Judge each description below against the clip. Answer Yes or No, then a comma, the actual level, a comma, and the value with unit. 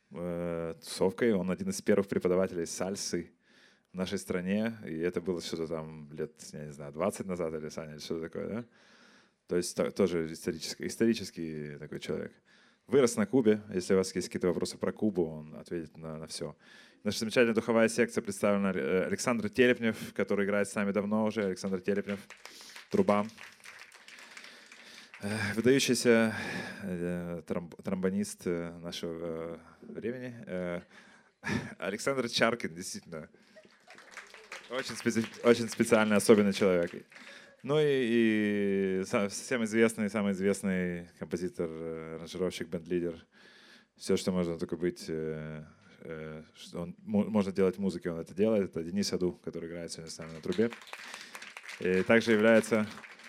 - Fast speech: No, average, 130 wpm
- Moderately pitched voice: No, very low, 95 Hz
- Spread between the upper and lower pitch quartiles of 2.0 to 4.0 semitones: No, average, 4.4 semitones